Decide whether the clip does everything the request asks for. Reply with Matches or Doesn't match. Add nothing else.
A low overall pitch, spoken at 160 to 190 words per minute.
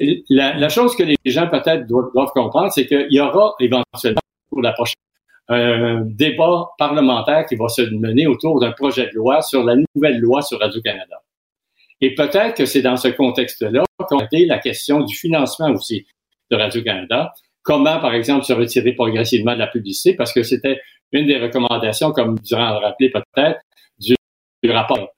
Matches